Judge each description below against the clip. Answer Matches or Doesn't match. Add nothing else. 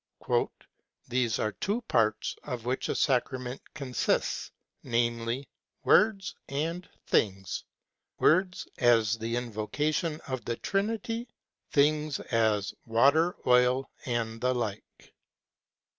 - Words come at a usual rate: Doesn't match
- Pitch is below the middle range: Matches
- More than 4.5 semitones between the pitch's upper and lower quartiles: Matches